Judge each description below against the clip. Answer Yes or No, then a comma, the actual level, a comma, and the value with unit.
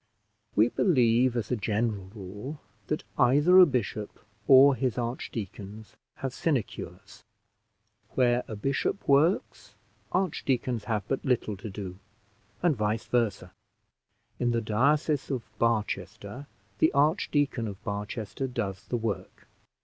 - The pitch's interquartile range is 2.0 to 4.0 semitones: No, average, 4.4 semitones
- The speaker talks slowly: Yes, slow, 120 wpm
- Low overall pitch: Yes, low, 120 Hz